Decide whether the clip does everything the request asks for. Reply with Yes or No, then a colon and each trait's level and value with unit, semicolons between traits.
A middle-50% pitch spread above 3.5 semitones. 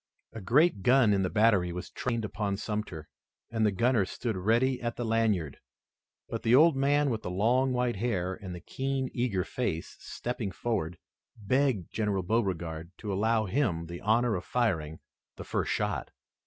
Yes: average, 4.9 semitones